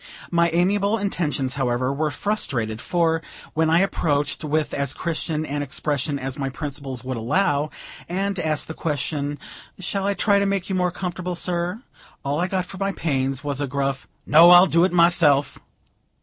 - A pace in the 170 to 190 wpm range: Yes, average, 175 wpm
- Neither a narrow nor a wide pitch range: Yes, average, 4.3 semitones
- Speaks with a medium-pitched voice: Yes, medium, 160 Hz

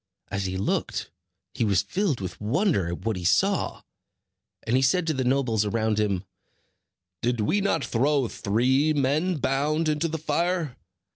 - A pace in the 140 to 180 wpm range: Yes, average, 160 wpm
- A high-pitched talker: No, low, 130 Hz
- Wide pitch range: Yes, wide, 6.5 semitones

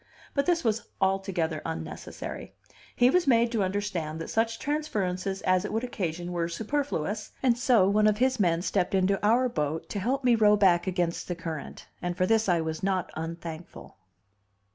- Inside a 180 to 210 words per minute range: Yes, average, 185 wpm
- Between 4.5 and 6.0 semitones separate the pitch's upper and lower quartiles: Yes, average, 4.8 semitones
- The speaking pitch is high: Yes, high, 195 Hz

